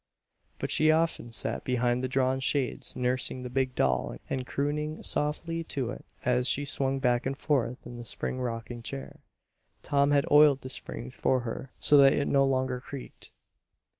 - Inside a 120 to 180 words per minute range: Yes, average, 175 wpm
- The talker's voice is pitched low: Yes, low, 130 Hz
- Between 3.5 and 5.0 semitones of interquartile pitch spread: No, narrow, 2.4 semitones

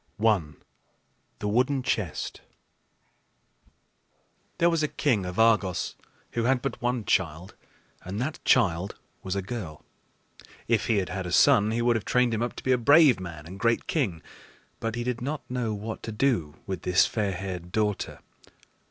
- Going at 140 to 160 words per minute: No, average, 170 wpm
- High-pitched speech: No, low, 110 Hz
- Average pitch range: Yes, average, 4.7 semitones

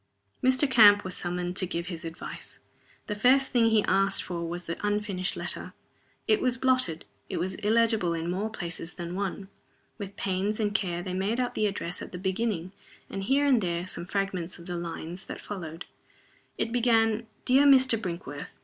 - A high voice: Yes, high, 195 Hz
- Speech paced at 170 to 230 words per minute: Yes, average, 185 wpm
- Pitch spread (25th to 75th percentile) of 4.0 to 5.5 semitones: Yes, average, 4.3 semitones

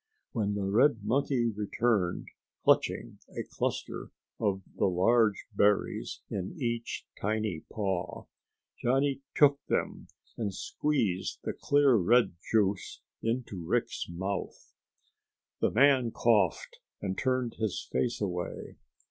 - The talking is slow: Yes, slow, 115 wpm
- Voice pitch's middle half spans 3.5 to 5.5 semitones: Yes, average, 4.1 semitones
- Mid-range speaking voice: No, low, 110 Hz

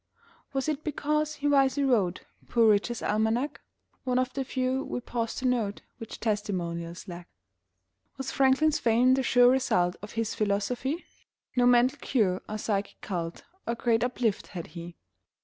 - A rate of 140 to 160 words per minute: Yes, average, 155 wpm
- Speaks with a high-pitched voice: Yes, high, 240 Hz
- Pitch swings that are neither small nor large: Yes, average, 4.3 semitones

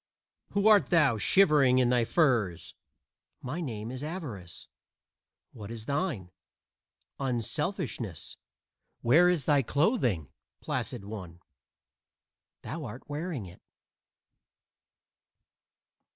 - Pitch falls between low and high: No, low, 130 Hz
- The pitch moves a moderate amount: No, wide, 6.6 semitones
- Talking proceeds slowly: Yes, slow, 95 wpm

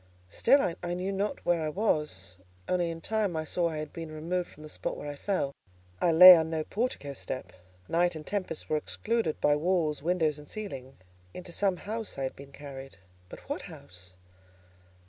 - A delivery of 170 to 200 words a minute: Yes, average, 185 wpm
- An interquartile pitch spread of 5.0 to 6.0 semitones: No, average, 3.9 semitones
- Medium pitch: Yes, medium, 160 Hz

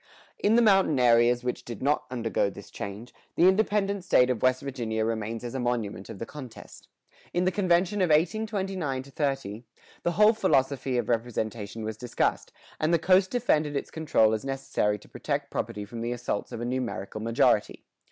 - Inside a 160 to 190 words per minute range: Yes, average, 180 wpm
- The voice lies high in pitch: No, low, 130 Hz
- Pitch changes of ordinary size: No, wide, 7.0 semitones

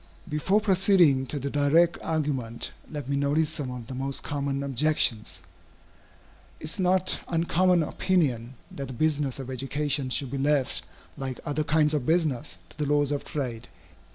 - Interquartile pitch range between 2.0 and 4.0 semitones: Yes, average, 2.9 semitones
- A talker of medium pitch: Yes, medium, 145 Hz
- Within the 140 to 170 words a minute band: Yes, average, 165 wpm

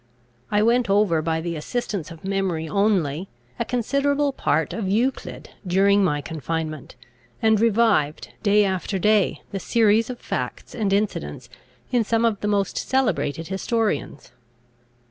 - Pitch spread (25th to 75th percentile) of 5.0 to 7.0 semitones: Yes, average, 5.3 semitones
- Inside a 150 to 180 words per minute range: No, average, 140 wpm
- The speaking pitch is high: Yes, high, 200 Hz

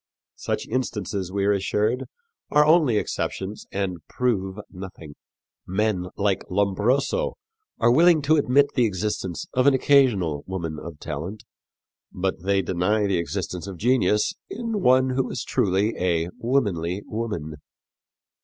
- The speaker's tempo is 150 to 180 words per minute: No, slow, 135 wpm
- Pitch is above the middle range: No, low, 100 Hz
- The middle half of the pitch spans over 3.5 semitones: Yes, wide, 5.5 semitones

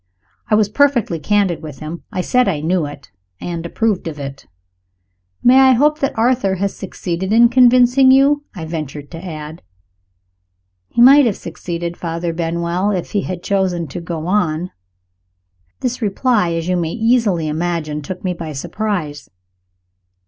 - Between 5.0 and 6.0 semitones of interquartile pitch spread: Yes, wide, 5.6 semitones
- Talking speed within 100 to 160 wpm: Yes, average, 155 wpm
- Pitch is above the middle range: No, medium, 180 Hz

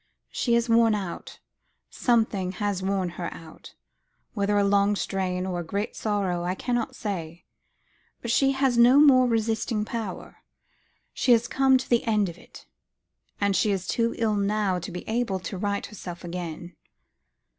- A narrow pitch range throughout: No, average, 4.0 semitones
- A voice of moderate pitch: No, high, 205 Hz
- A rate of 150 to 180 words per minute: Yes, average, 165 wpm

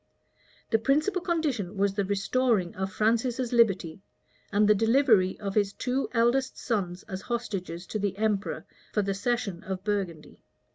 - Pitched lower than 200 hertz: No, high, 210 Hz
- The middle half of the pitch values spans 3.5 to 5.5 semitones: Yes, average, 3.8 semitones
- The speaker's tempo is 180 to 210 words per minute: No, average, 150 wpm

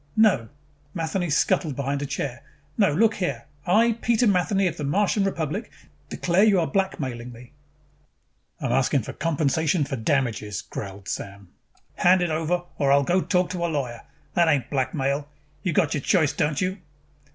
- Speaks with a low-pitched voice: No, medium, 155 Hz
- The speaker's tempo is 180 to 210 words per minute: No, average, 165 wpm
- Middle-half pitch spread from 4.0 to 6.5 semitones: Yes, wide, 5.4 semitones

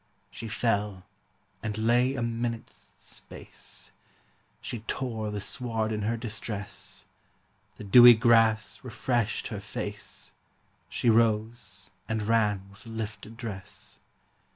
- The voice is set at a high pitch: No, low, 110 Hz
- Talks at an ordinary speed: No, slow, 110 wpm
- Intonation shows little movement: Yes, narrow, 1.9 semitones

